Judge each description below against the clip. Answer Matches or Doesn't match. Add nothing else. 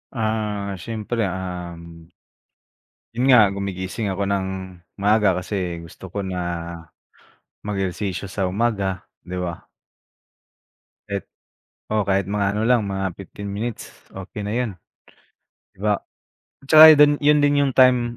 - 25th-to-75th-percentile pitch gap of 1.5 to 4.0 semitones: Matches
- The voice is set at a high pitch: Doesn't match